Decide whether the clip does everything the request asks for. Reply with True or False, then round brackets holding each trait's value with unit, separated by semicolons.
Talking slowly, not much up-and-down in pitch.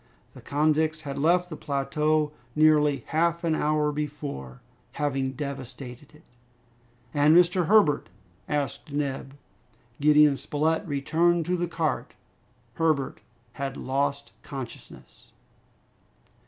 True (105 wpm; 2.2 semitones)